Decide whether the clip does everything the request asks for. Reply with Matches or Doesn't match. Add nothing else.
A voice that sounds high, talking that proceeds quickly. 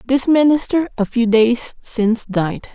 Doesn't match